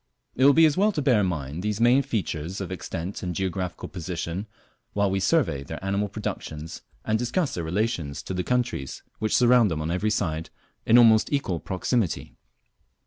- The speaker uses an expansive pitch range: Yes, wide, 5.7 semitones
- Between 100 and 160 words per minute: No, average, 185 wpm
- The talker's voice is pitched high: No, low, 100 Hz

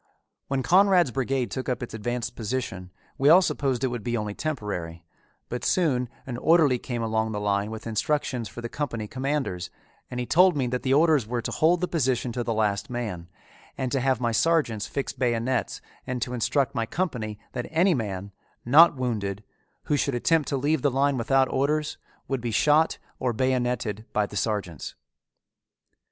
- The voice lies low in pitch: Yes, low, 125 Hz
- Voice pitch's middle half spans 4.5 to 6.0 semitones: No, average, 4.1 semitones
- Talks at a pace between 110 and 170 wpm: No, average, 185 wpm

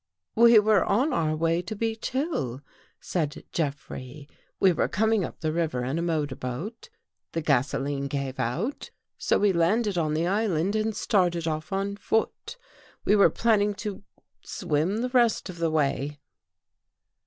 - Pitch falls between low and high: Yes, medium, 170 Hz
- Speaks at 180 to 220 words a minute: No, average, 170 wpm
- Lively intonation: Yes, wide, 6.0 semitones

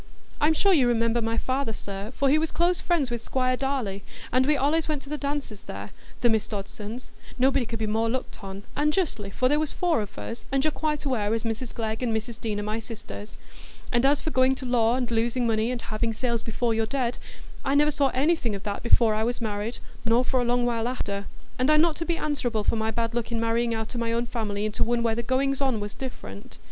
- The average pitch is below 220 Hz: No, high, 235 Hz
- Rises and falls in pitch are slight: No, average, 3.5 semitones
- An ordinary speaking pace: No, fast, 240 wpm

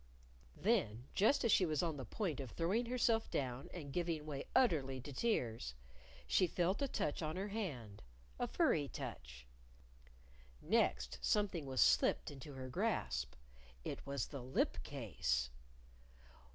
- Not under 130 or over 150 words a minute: Yes, average, 145 wpm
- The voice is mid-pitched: Yes, medium, 145 Hz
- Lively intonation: Yes, wide, 7.0 semitones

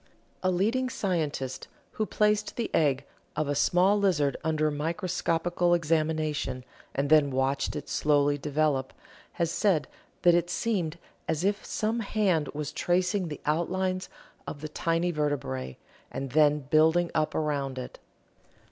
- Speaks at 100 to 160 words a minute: Yes, average, 140 wpm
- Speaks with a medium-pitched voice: Yes, medium, 155 Hz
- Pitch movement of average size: Yes, average, 3.8 semitones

